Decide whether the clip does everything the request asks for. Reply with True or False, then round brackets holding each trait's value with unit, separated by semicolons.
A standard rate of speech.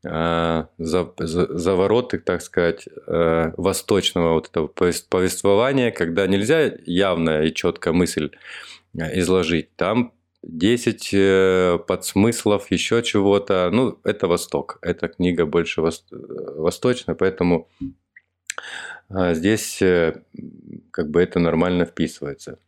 False (85 wpm)